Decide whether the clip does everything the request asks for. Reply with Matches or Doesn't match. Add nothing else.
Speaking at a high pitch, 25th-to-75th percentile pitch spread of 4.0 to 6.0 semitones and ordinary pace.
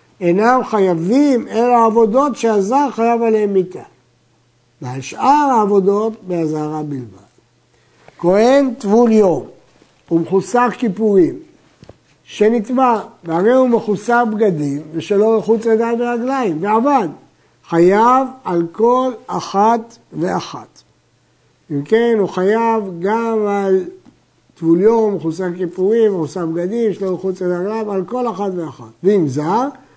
Matches